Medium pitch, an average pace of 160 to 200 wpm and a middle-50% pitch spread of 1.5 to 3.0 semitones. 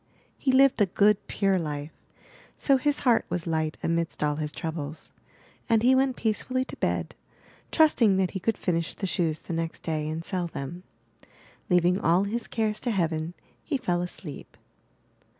No: medium, 180 Hz; average, 170 wpm; wide, 5.6 semitones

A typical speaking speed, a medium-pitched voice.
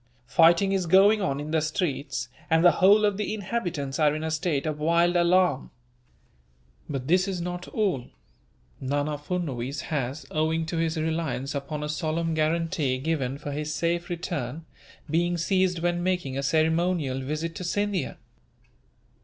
Yes: average, 155 wpm; medium, 160 Hz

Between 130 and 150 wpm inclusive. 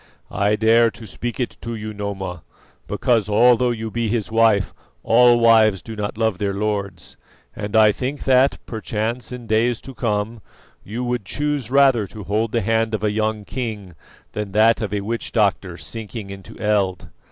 No: average, 175 wpm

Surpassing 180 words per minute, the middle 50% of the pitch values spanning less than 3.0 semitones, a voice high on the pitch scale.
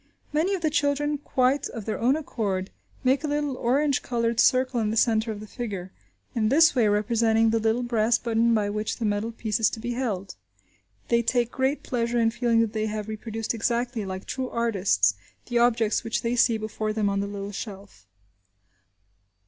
Yes: average, 195 wpm; narrow, 2.5 semitones; high, 230 Hz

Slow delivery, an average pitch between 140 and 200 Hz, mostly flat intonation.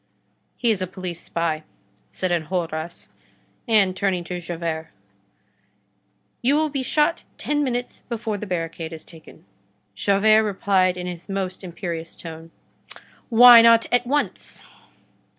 No: slow, 130 wpm; medium, 185 Hz; average, 5.3 semitones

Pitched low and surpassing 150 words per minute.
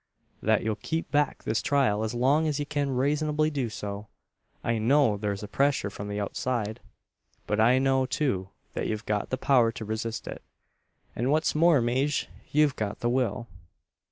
Yes: low, 125 Hz; average, 175 wpm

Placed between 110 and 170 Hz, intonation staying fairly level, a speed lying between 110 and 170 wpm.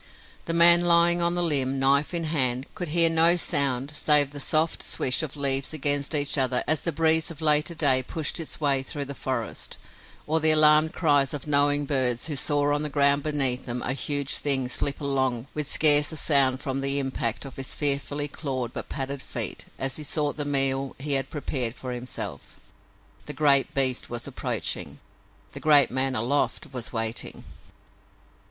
No: medium, 140 Hz; narrow, 2.3 semitones; average, 185 wpm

